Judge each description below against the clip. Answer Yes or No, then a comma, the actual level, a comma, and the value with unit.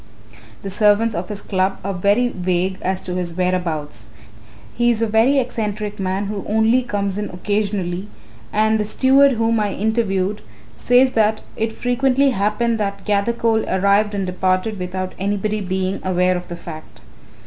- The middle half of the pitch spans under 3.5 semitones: Yes, average, 3.0 semitones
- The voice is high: Yes, high, 205 Hz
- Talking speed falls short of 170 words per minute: Yes, average, 160 wpm